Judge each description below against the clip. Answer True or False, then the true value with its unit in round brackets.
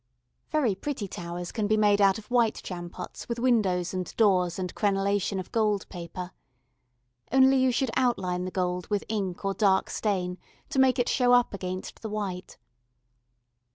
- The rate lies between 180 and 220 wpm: False (165 wpm)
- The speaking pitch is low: False (200 Hz)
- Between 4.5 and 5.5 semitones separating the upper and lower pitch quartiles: False (4.1 semitones)